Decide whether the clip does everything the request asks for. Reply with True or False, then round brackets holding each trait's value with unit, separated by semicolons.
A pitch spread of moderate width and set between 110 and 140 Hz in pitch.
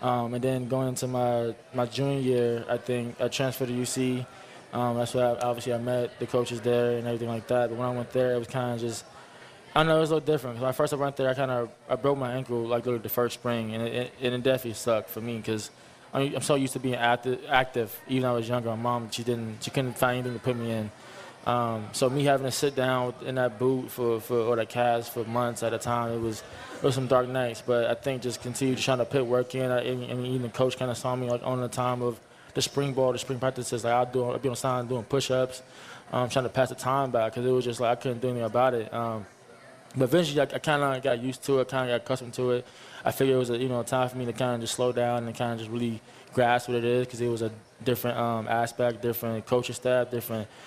False (1.5 semitones; 125 Hz)